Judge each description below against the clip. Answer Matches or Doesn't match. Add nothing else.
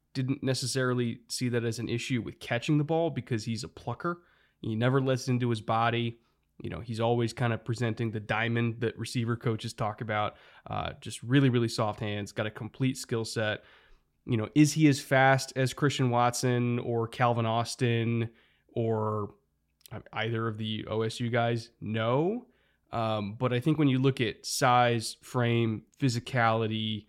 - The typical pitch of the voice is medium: Doesn't match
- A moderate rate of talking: Matches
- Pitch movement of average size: Doesn't match